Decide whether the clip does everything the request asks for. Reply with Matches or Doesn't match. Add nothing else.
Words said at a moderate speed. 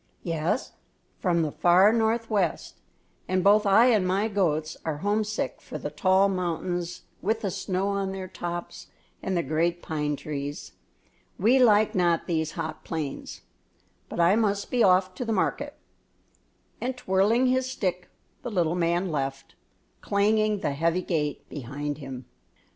Matches